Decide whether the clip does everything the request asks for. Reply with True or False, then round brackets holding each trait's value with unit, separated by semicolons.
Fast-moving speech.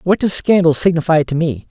True (210 wpm)